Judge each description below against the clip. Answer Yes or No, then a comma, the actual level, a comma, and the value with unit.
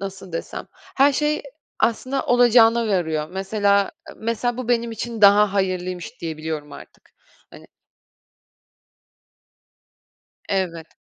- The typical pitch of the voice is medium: No, high, 200 Hz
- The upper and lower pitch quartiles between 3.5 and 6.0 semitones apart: Yes, average, 4.5 semitones